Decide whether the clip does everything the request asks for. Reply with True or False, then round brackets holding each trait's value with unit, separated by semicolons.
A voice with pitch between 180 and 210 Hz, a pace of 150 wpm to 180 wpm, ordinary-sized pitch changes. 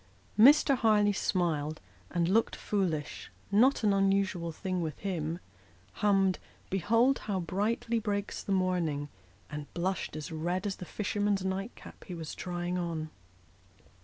False (190 Hz; 140 wpm; 3.4 semitones)